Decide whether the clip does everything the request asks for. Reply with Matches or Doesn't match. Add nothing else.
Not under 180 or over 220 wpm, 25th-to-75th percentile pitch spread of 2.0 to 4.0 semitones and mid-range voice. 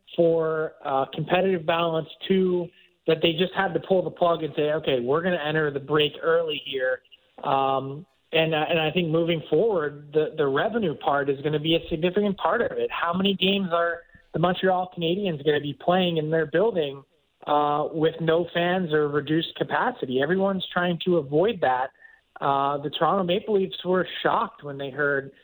Matches